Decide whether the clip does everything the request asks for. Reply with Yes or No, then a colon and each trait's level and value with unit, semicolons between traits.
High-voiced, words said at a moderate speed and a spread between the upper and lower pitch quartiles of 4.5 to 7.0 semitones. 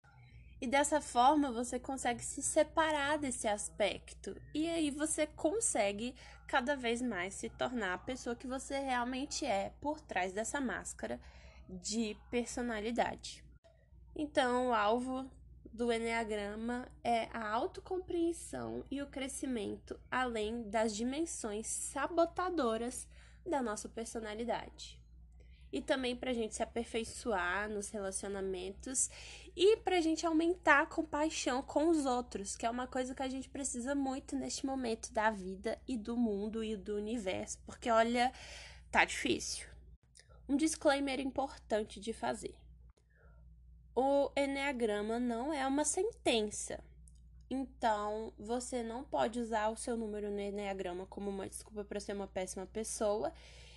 Yes: high, 240 Hz; average, 130 wpm; average, 4.9 semitones